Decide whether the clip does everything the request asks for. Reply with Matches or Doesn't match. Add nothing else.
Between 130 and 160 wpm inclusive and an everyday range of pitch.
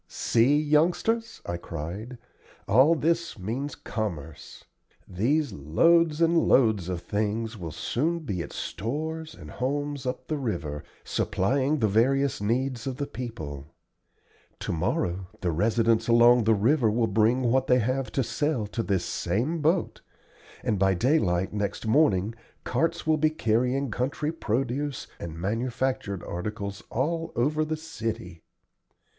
Doesn't match